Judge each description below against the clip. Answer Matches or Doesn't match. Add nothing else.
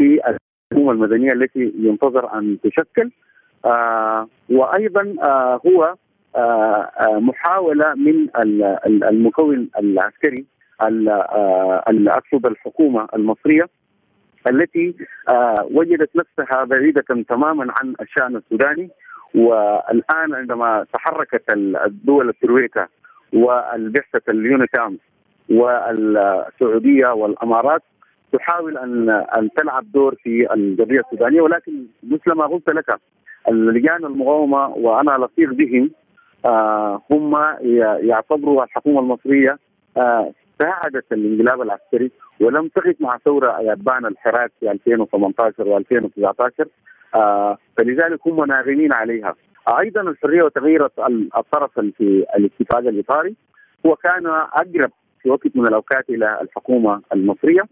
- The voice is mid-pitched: Doesn't match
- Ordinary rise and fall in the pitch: Doesn't match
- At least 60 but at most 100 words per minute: Matches